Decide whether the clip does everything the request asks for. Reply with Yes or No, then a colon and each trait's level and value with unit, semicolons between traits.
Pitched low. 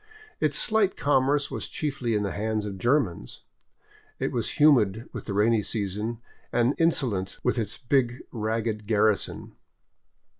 Yes: low, 115 Hz